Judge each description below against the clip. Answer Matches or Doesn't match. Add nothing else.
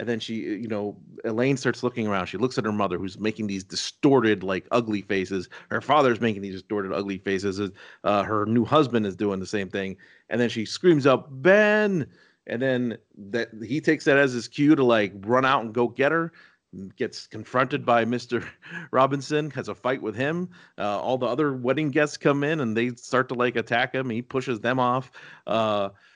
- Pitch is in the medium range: Doesn't match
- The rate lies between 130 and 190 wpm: Doesn't match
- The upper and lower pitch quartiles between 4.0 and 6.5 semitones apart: Matches